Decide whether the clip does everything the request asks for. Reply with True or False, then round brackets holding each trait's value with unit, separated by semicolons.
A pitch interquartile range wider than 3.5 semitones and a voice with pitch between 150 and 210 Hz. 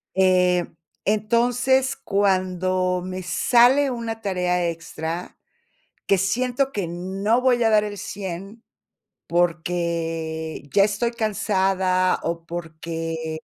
True (4.0 semitones; 185 Hz)